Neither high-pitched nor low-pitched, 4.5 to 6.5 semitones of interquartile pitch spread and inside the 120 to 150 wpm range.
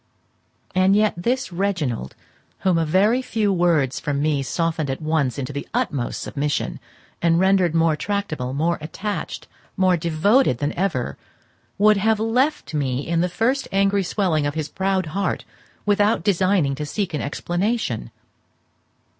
Yes: medium, 175 Hz; average, 5.2 semitones; average, 145 wpm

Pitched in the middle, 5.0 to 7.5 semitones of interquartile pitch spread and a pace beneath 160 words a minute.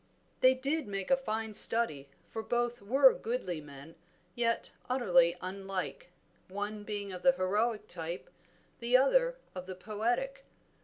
No: high, 215 Hz; wide, 5.4 semitones; average, 140 wpm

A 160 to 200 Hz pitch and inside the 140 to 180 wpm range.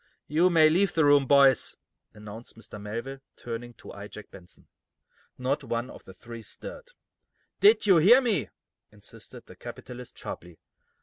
No: low, 130 Hz; average, 150 wpm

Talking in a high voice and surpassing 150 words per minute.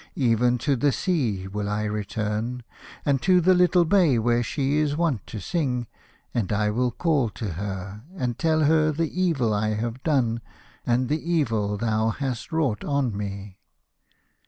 No: low, 120 Hz; average, 165 wpm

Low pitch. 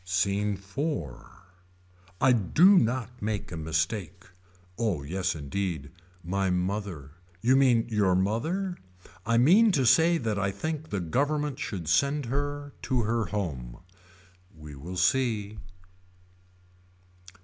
Yes: low, 105 Hz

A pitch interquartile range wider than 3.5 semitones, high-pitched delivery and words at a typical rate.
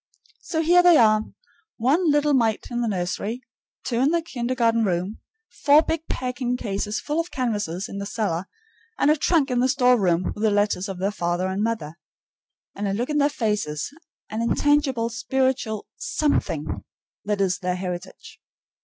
Yes: wide, 5.5 semitones; high, 230 Hz; average, 170 wpm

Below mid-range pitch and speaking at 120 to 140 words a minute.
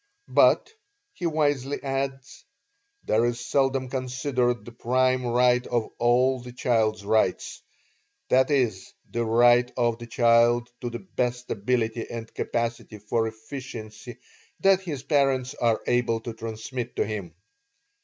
Yes: low, 120 Hz; slow, 135 wpm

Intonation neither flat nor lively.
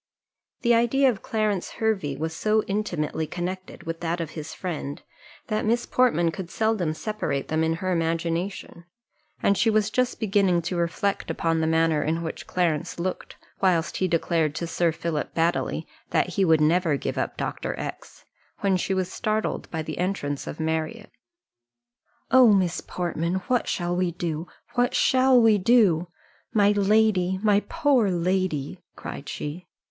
Yes: average, 4.6 semitones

